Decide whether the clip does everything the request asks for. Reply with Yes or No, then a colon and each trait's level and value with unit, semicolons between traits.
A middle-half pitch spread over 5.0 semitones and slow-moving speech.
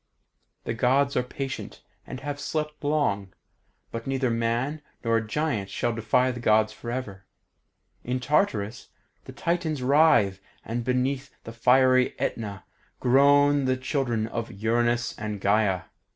No: average, 3.5 semitones; slow, 130 wpm